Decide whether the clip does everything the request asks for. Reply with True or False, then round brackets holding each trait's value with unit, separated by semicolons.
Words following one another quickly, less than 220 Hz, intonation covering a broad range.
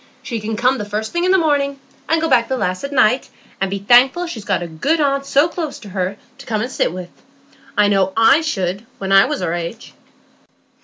False (235 wpm; 230 Hz; 6.2 semitones)